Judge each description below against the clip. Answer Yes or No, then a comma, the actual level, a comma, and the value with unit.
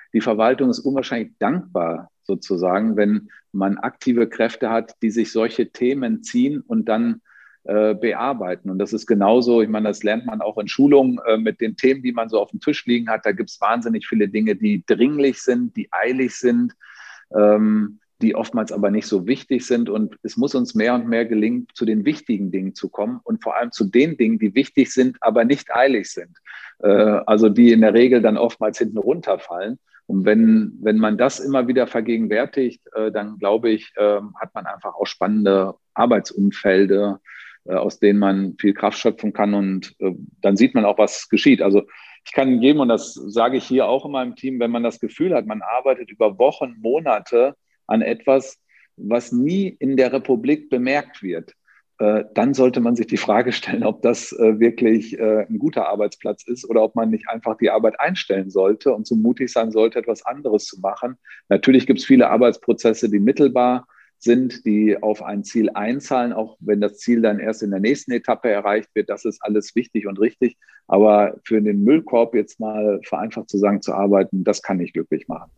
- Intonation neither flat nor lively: Yes, average, 3.6 semitones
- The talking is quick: Yes, fast, 195 wpm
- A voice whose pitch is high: No, low, 115 Hz